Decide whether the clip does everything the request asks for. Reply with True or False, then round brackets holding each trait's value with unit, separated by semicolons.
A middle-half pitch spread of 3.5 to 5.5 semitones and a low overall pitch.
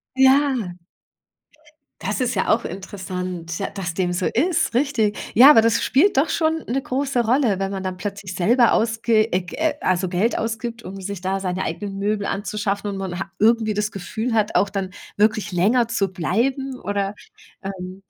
False (3.9 semitones; 210 Hz)